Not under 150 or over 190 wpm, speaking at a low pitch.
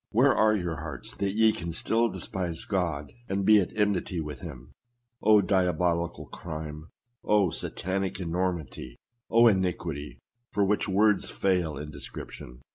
No: average, 140 wpm; very low, 90 Hz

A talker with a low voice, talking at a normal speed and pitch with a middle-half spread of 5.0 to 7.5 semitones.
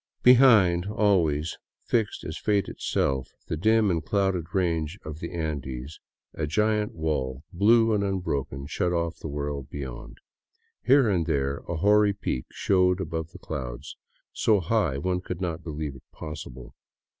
Yes: very low, 85 Hz; average, 150 wpm; wide, 5.4 semitones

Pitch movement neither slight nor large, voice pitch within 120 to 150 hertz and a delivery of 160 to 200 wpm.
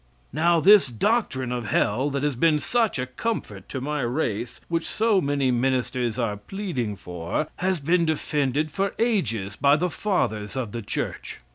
No: wide, 6.3 semitones; medium, 140 Hz; average, 165 wpm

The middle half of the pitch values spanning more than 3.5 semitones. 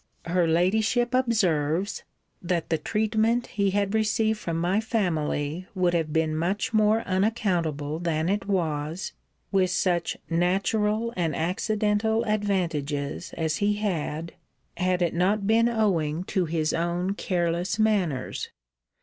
Yes: average, 4.3 semitones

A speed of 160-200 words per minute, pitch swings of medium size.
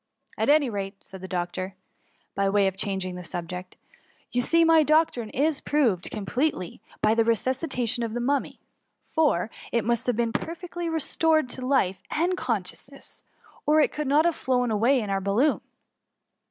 No: average, 180 wpm; wide, 7.2 semitones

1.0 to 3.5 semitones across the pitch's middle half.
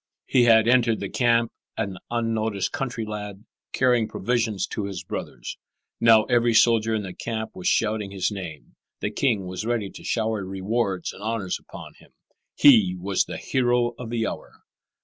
Yes: average, 3.0 semitones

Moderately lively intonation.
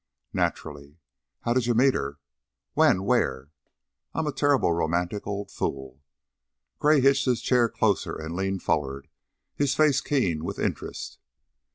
No: wide, 8.9 semitones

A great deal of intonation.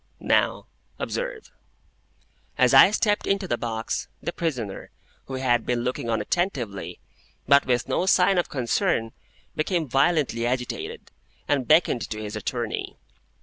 Yes: wide, 6.8 semitones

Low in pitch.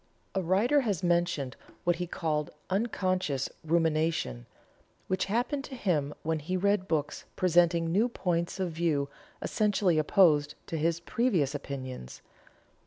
No: medium, 170 Hz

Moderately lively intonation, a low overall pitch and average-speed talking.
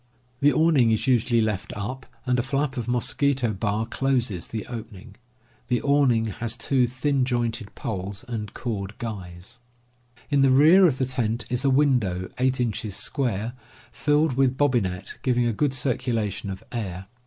Yes: average, 3.6 semitones; low, 120 Hz; average, 160 wpm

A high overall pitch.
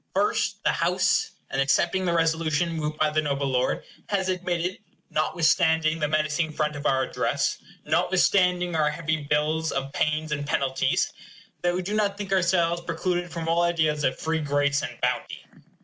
No: medium, 160 Hz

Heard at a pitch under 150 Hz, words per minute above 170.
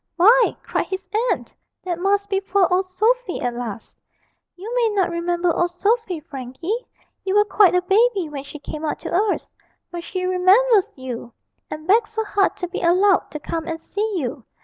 No: very high, 370 Hz; average, 190 wpm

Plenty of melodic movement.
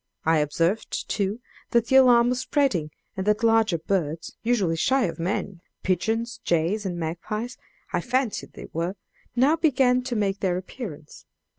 Yes: wide, 6.0 semitones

